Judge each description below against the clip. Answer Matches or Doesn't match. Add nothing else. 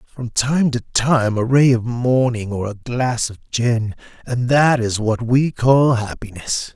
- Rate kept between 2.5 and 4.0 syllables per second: Matches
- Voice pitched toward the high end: Doesn't match